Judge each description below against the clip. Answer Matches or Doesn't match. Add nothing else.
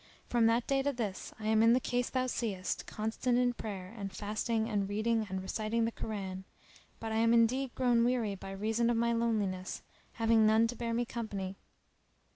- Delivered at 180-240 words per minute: Matches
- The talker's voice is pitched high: Matches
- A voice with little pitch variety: Matches